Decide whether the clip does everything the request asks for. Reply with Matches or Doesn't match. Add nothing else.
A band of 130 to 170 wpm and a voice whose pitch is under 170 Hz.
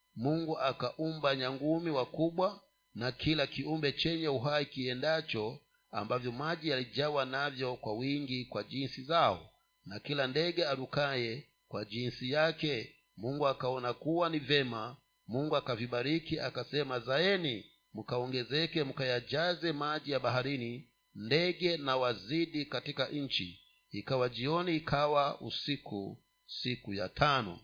Doesn't match